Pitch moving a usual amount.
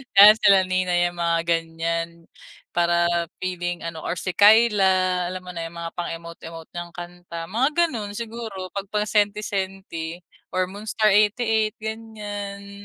Yes: average, 3.4 semitones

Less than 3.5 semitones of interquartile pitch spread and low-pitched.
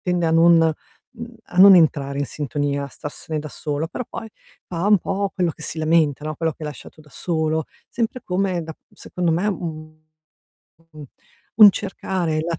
No: average, 2.7 semitones; medium, 165 Hz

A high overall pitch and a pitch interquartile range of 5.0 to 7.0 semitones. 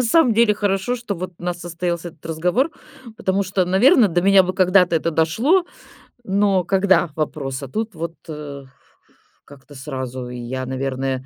No: medium, 175 Hz; wide, 5.4 semitones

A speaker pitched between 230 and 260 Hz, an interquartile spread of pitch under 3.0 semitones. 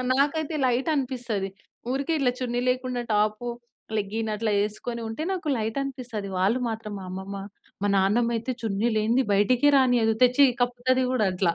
No: high, 240 Hz; average, 3.4 semitones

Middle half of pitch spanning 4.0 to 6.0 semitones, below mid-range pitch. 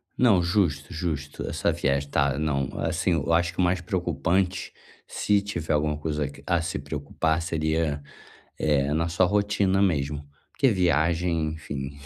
No: average, 3.5 semitones; very low, 80 Hz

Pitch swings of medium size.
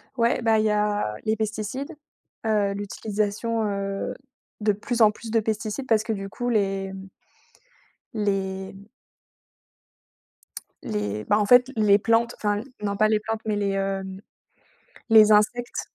No: narrow, 1.9 semitones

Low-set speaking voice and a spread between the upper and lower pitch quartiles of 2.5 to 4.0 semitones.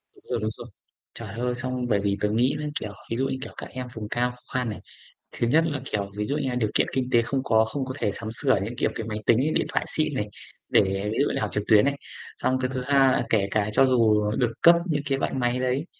Yes: low, 125 Hz; average, 3.5 semitones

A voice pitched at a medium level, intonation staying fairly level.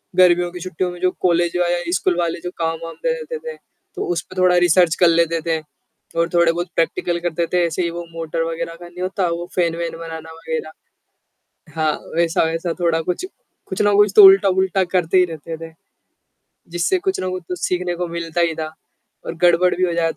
Yes: medium, 175 Hz; narrow, 1.6 semitones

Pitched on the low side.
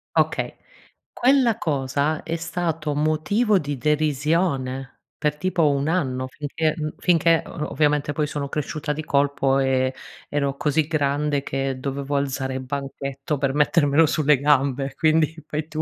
No: medium, 145 Hz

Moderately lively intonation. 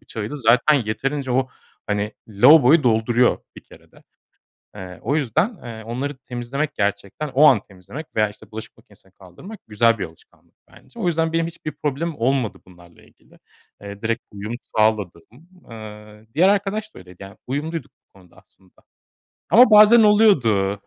No: wide, 6.8 semitones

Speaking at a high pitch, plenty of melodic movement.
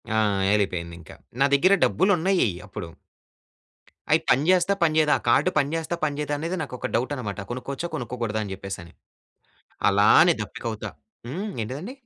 No: medium, 140 Hz; wide, 7.8 semitones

